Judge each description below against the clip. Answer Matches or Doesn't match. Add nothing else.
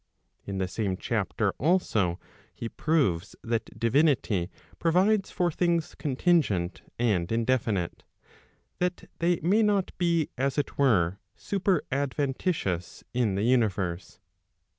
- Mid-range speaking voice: Doesn't match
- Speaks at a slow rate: Matches